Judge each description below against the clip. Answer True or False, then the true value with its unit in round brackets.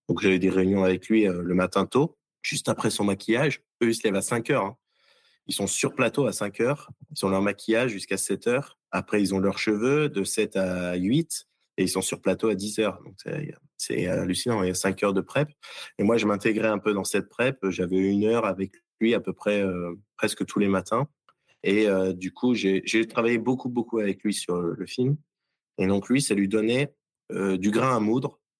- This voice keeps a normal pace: False (235 wpm)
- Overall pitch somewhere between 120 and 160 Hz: False (105 Hz)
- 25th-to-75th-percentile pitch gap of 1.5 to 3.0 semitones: False (3.7 semitones)